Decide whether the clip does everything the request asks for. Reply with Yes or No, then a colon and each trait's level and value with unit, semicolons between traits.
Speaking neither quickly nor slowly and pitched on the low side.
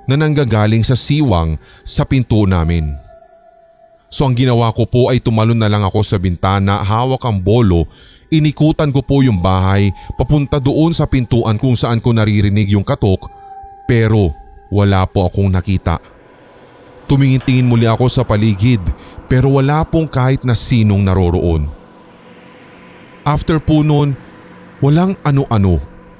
Yes: average, 135 wpm; low, 120 Hz